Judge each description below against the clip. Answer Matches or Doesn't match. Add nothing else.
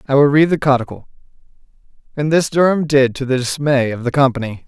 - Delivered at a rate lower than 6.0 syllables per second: Doesn't match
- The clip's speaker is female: Doesn't match